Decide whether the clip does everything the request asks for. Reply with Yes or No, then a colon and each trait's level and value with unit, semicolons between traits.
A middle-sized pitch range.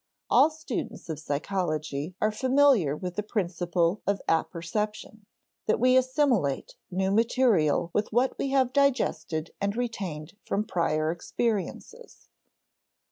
No: wide, 6.7 semitones